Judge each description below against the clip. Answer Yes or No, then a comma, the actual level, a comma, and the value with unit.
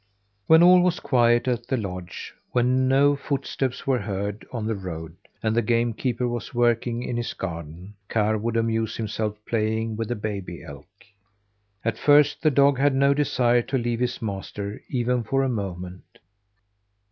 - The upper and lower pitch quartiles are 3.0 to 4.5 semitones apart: Yes, average, 3.5 semitones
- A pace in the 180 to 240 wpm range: No, average, 170 wpm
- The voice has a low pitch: Yes, low, 115 Hz